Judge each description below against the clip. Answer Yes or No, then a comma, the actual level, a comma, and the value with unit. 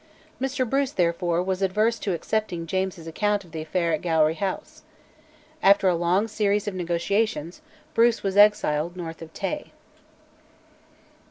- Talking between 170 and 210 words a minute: No, average, 145 wpm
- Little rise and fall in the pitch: No, average, 3.7 semitones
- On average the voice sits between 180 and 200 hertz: Yes, high, 190 Hz